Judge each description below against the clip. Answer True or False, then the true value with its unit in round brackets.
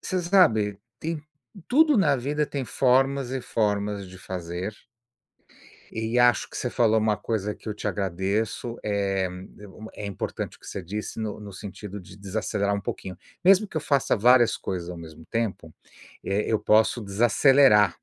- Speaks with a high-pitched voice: False (105 Hz)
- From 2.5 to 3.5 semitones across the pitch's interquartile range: False (3.9 semitones)